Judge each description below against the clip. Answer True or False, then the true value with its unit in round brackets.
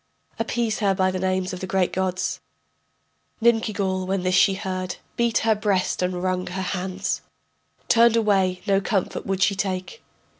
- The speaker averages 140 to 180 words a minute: True (160 wpm)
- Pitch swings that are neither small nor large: False (2.1 semitones)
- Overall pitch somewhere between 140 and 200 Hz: True (190 Hz)